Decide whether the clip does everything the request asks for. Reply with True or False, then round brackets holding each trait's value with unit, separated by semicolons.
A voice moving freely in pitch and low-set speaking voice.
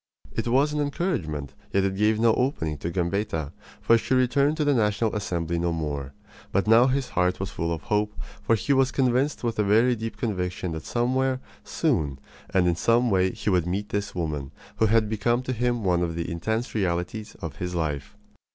True (5.9 semitones; 105 Hz)